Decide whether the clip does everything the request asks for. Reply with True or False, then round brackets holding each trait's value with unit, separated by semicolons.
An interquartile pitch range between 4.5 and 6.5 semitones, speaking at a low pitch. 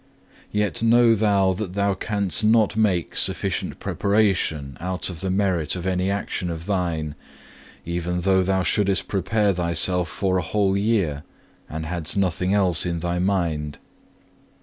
False (2.7 semitones; 95 Hz)